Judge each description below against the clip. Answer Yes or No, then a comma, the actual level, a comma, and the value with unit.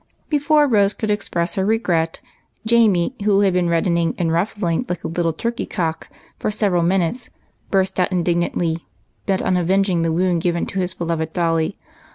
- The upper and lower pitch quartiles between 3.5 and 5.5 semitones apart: No, average, 3.1 semitones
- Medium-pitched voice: Yes, medium, 180 Hz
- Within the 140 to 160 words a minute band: No, average, 170 wpm